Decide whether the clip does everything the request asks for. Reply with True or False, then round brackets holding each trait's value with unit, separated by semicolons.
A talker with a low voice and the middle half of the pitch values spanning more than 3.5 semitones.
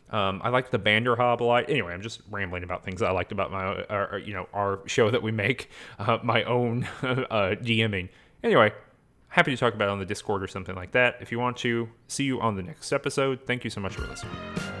True (115 Hz; 3.9 semitones)